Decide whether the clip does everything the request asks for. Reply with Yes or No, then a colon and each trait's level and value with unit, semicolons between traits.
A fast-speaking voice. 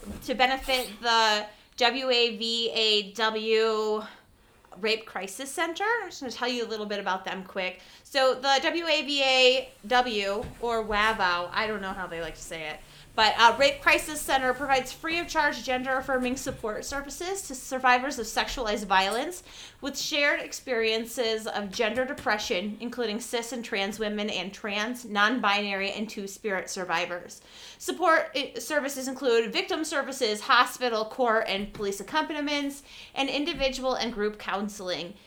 No: average, 145 wpm